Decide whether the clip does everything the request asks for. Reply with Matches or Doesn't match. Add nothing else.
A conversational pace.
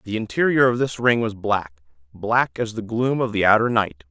Doesn't match